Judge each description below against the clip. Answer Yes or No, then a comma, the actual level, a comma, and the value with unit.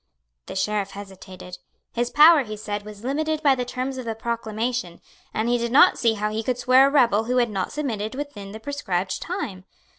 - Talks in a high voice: Yes, high, 230 Hz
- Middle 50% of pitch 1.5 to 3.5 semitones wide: No, average, 4.0 semitones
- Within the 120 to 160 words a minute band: No, fast, 205 wpm